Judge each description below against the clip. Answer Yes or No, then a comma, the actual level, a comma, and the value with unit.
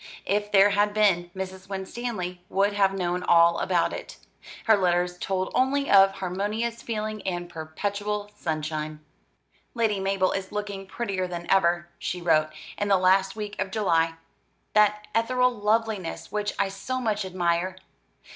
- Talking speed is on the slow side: No, average, 145 wpm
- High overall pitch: Yes, high, 195 Hz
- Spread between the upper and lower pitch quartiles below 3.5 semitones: Yes, average, 2.8 semitones